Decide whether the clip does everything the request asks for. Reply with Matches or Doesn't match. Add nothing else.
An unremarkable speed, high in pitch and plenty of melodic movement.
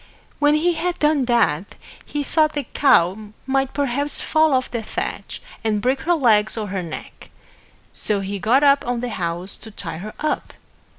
Matches